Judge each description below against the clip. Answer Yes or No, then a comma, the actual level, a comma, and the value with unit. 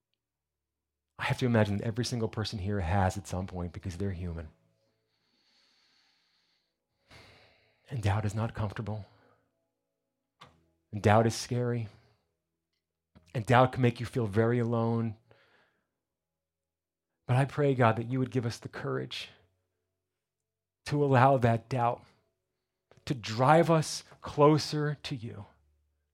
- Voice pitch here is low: Yes, low, 110 Hz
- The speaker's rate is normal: No, slow, 125 wpm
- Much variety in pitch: Yes, wide, 6.3 semitones